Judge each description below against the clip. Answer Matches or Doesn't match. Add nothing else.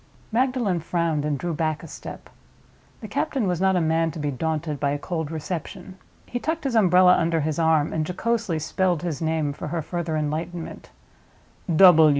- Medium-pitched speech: Matches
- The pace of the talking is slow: Doesn't match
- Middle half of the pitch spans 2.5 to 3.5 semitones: Matches